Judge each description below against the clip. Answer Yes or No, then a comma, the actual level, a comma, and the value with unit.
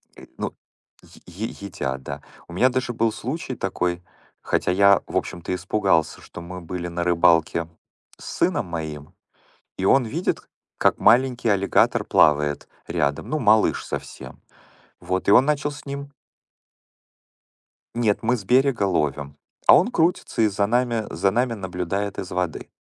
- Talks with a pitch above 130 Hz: No, low, 100 Hz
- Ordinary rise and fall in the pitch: No, wide, 5.9 semitones